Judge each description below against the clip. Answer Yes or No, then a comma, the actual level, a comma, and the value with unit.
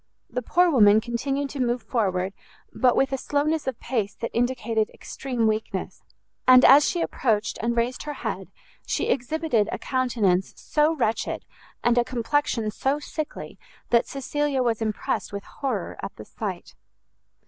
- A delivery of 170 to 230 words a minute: No, average, 155 wpm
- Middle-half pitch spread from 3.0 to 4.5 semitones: Yes, average, 3.8 semitones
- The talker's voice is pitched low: No, high, 245 Hz